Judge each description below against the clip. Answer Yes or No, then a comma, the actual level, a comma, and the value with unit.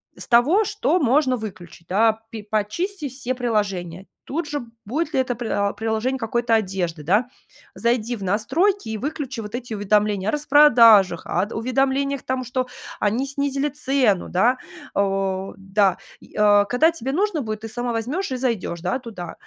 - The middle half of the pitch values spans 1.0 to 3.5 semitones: No, average, 4.7 semitones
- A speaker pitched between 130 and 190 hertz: No, high, 235 Hz